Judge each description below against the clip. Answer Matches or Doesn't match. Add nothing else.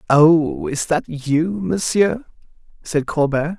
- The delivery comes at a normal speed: Doesn't match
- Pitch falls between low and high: Matches